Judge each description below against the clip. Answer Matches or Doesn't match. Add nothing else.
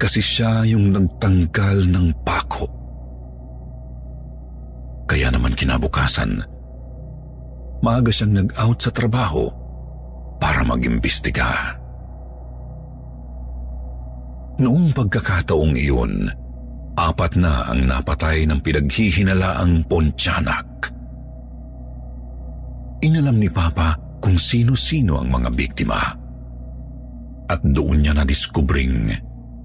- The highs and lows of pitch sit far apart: Matches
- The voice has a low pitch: Matches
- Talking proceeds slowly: Matches